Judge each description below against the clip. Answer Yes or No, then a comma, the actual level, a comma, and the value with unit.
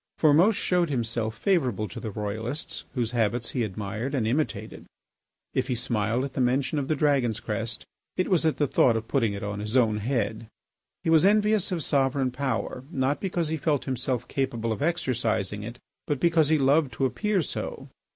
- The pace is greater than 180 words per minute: Yes, average, 190 wpm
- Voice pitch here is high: No, low, 130 Hz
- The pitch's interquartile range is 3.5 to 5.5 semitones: Yes, average, 5.2 semitones